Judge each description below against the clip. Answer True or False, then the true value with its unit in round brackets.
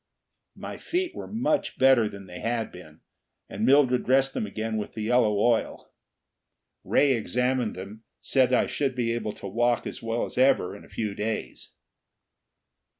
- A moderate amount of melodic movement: True (3.5 semitones)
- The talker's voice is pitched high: False (115 Hz)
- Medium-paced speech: True (170 wpm)